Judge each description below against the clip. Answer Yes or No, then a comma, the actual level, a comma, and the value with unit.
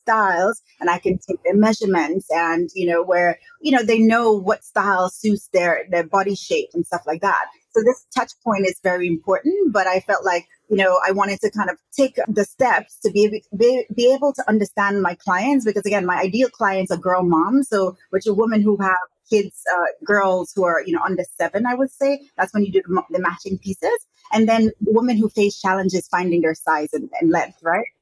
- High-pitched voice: Yes, high, 200 Hz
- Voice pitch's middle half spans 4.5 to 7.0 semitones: No, average, 3.5 semitones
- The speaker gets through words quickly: Yes, fast, 225 wpm